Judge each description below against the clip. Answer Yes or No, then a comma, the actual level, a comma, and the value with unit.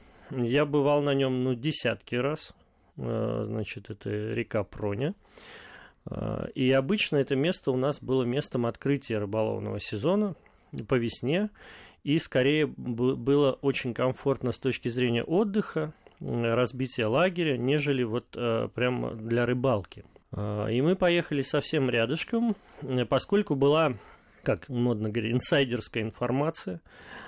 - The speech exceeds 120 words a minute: No, average, 115 wpm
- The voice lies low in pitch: Yes, low, 130 Hz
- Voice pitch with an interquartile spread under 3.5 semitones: No, average, 3.9 semitones